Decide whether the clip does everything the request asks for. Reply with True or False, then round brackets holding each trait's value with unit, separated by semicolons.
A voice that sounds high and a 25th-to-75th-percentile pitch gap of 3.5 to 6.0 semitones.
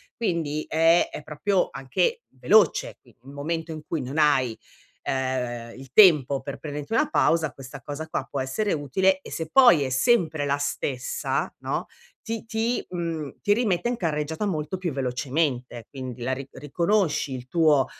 False (150 Hz; 4.8 semitones)